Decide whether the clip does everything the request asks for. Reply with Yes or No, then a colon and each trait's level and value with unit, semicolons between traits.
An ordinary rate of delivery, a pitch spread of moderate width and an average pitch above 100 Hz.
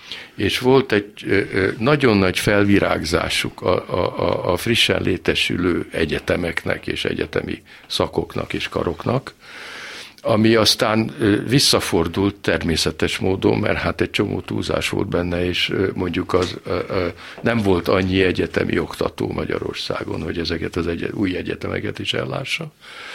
No: average, 125 wpm; average, 3.7 semitones; very low, 95 Hz